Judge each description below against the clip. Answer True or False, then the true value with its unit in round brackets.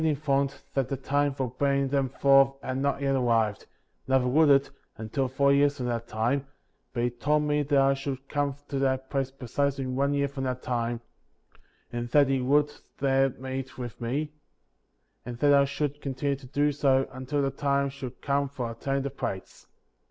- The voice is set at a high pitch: False (135 Hz)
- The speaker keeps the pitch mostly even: True (1.6 semitones)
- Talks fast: False (190 wpm)